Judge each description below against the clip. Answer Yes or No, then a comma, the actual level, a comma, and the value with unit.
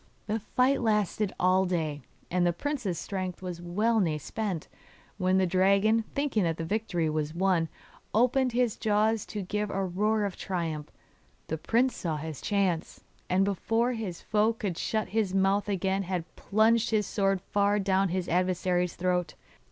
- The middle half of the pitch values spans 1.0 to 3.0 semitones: No, average, 3.4 semitones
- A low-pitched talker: No, high, 195 Hz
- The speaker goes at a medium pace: Yes, average, 165 wpm